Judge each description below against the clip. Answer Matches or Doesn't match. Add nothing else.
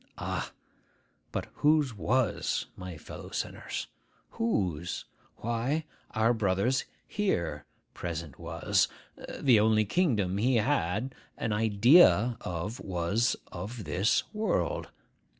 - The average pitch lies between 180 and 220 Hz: Doesn't match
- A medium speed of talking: Doesn't match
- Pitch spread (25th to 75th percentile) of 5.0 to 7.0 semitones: Matches